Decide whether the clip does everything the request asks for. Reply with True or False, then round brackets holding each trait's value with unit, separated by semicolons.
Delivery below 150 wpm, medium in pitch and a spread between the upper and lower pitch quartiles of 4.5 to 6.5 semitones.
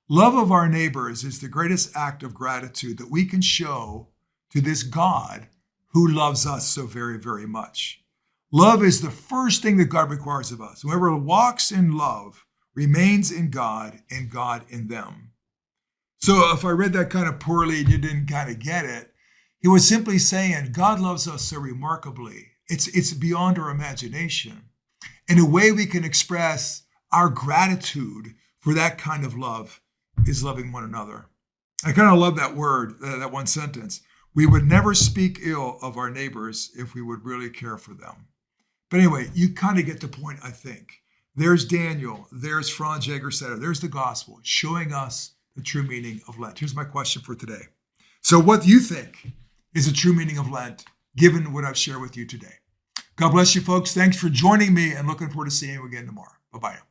False (190 wpm; 150 Hz; 5.4 semitones)